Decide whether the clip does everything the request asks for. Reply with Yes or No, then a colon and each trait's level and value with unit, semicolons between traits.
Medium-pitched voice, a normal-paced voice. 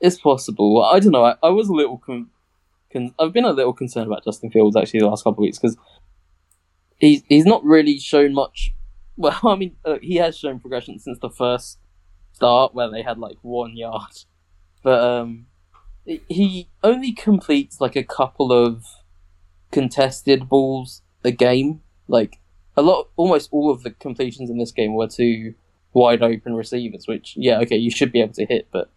No: low, 120 Hz; average, 190 wpm